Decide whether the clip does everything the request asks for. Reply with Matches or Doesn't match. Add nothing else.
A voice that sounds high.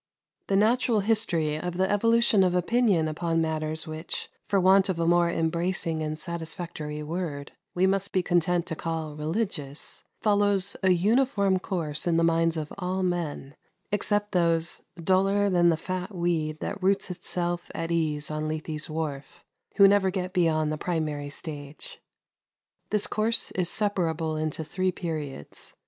Doesn't match